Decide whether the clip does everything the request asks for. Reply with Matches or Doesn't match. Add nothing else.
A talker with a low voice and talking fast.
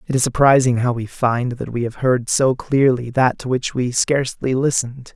Matches